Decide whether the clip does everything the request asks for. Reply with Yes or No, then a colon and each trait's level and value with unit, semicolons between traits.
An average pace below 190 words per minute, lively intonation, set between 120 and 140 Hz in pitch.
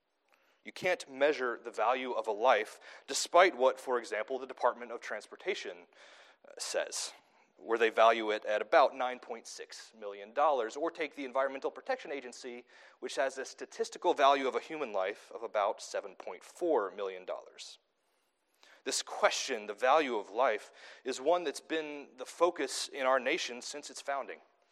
Yes: average, 150 wpm; wide, 6.0 semitones; low, 135 Hz